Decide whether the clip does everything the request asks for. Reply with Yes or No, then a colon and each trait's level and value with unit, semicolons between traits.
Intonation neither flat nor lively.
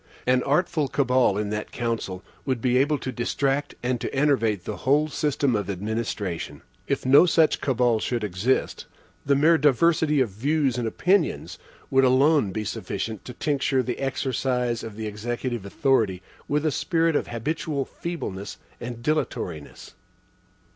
Yes: average, 4.6 semitones